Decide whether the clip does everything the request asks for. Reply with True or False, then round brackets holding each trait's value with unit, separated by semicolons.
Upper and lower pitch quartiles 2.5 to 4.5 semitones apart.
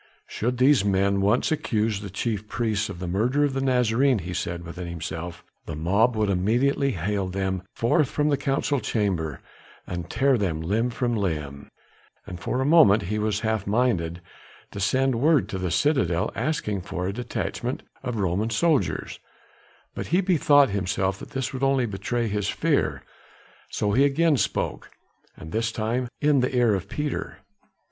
False (5.5 semitones)